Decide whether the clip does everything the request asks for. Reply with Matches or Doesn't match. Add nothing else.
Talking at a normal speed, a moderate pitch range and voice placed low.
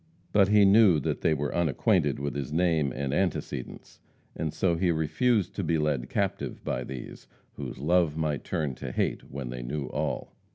Matches